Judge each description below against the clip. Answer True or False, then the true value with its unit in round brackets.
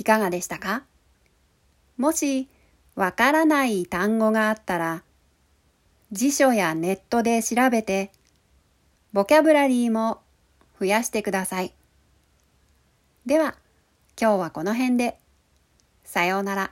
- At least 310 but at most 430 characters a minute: False (225 characters per minute)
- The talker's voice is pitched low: False (200 Hz)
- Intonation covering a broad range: True (6.6 semitones)